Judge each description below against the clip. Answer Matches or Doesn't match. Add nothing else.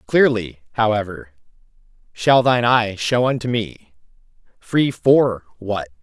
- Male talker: Matches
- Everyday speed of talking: Doesn't match